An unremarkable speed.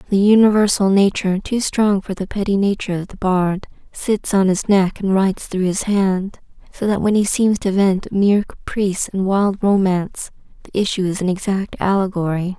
Yes: average, 190 wpm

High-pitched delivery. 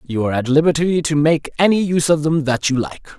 No: medium, 150 Hz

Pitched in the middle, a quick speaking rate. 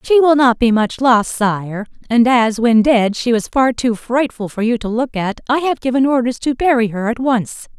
No: high, 240 Hz; fast, 230 wpm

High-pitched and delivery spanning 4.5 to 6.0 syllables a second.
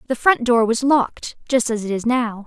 Yes: high, 235 Hz; 5.1 syllables/s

